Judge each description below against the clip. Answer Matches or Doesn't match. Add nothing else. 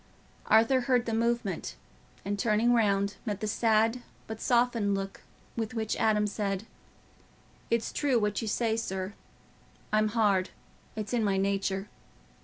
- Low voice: Doesn't match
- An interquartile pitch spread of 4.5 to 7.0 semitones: Doesn't match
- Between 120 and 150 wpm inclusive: Matches